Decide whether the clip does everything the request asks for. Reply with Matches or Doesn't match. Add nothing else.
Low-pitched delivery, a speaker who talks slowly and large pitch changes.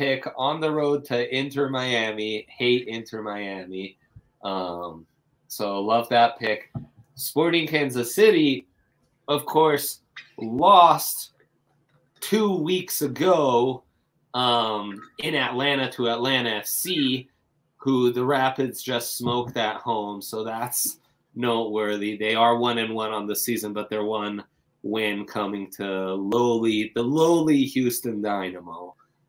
Doesn't match